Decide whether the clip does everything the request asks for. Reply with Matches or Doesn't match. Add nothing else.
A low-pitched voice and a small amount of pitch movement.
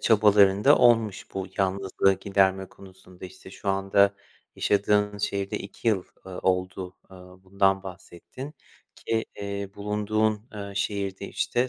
Matches